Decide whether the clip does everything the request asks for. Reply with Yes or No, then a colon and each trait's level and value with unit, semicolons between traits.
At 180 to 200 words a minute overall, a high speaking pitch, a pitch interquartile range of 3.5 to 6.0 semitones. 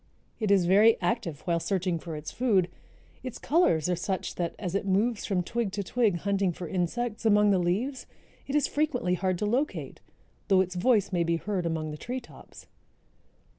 Yes: average, 190 wpm; high, 195 Hz; average, 4.5 semitones